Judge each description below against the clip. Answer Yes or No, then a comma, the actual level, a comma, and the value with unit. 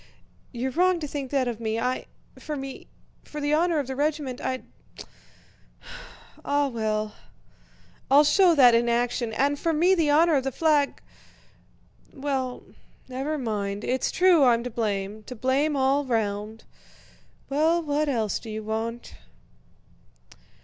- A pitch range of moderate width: Yes, average, 4.2 semitones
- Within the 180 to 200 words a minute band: No, average, 145 wpm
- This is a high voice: Yes, very high, 265 Hz